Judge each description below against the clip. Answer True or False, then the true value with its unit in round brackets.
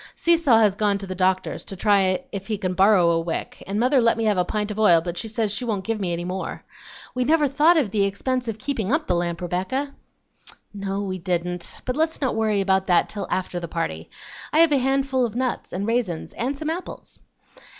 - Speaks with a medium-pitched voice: False (210 Hz)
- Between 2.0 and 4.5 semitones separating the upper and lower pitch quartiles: False (5.4 semitones)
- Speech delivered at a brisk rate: True (230 wpm)